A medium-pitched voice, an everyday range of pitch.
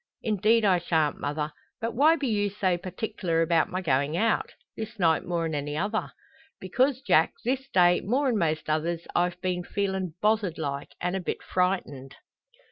Yes: medium, 180 Hz; average, 4.7 semitones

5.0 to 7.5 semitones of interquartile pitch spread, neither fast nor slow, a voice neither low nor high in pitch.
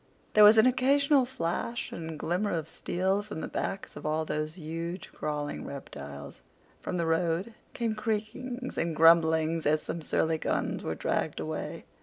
Yes: average, 5.3 semitones; average, 160 wpm; medium, 170 Hz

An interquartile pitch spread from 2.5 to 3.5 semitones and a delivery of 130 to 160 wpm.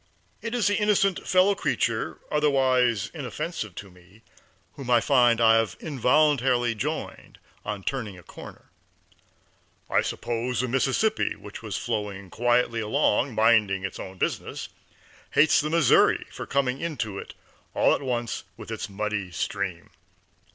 No: average, 4.9 semitones; average, 140 wpm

